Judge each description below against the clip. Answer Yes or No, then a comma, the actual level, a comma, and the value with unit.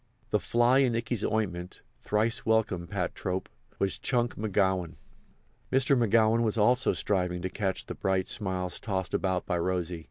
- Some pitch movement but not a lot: Yes, average, 3.9 semitones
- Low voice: Yes, low, 100 Hz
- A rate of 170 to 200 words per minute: No, average, 155 wpm